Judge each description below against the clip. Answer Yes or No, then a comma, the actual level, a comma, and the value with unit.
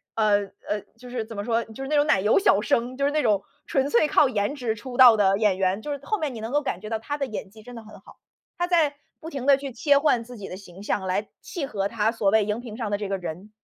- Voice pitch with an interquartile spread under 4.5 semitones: No, average, 5.0 semitones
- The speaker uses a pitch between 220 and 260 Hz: Yes, high, 225 Hz